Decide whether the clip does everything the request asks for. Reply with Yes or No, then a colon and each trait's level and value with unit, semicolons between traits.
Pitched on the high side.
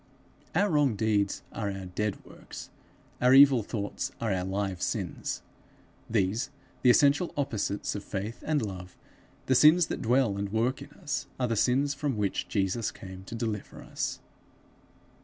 No: low, 110 Hz